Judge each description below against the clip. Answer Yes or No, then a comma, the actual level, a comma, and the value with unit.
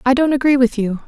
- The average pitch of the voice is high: Yes, very high, 255 Hz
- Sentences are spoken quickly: Yes, fast, 280 wpm